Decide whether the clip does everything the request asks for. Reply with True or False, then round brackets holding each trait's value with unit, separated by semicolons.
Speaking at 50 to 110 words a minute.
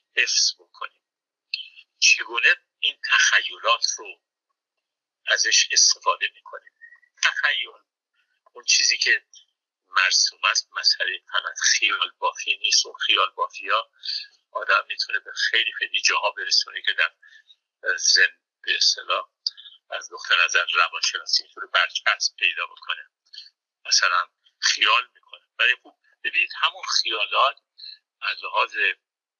True (105 wpm)